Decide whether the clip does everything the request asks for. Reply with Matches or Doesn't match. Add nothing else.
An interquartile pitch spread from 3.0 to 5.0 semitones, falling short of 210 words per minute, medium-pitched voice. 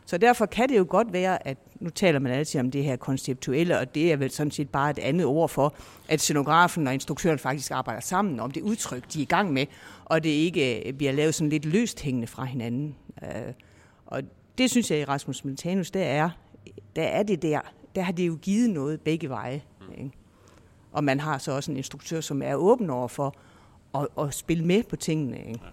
Doesn't match